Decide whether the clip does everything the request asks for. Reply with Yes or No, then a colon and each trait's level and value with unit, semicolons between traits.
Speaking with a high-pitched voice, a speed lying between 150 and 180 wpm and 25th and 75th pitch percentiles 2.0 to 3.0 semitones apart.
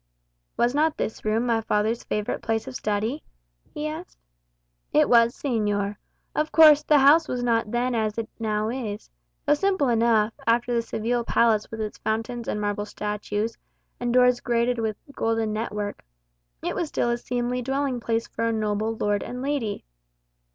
Yes: high, 230 Hz; average, 170 wpm; narrow, 2.6 semitones